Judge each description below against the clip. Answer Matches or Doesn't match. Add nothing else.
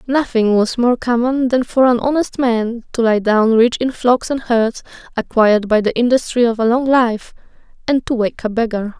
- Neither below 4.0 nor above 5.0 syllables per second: Matches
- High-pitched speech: Matches